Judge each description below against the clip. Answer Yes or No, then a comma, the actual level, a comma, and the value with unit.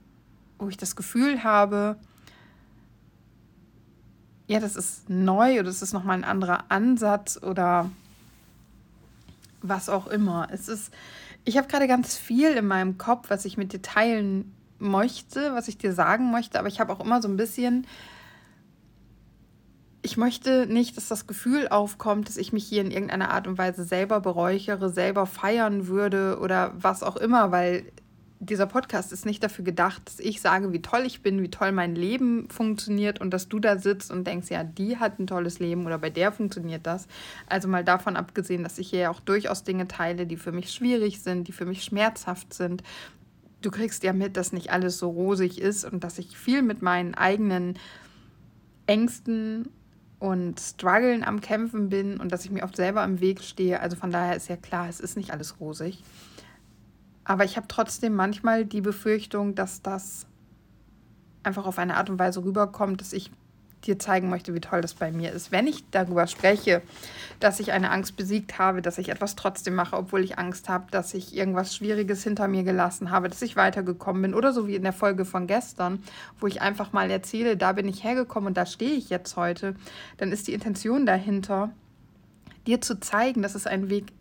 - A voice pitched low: No, high, 195 Hz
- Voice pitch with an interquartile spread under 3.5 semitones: Yes, narrow, 2.5 semitones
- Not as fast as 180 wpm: No, fast, 190 wpm